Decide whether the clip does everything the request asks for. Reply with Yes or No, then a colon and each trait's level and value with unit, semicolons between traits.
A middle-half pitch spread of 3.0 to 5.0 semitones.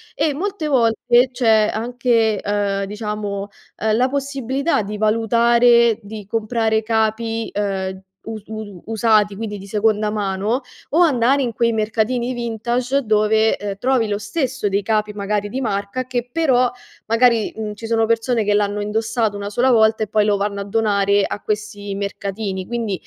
No: narrow, 2.4 semitones